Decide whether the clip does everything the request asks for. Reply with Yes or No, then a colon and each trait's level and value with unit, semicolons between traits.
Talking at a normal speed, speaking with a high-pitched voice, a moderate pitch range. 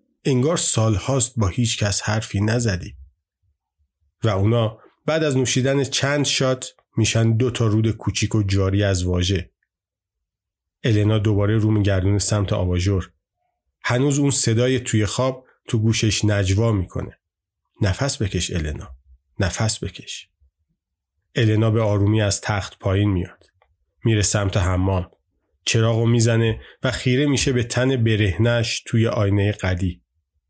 No: average, 130 wpm; low, 105 Hz; average, 3.8 semitones